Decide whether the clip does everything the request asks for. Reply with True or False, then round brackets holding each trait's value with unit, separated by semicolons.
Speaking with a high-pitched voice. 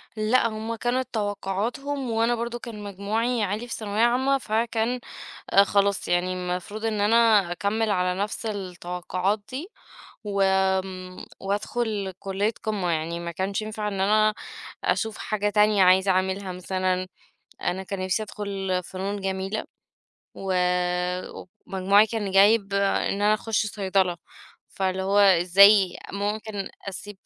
True (200 Hz)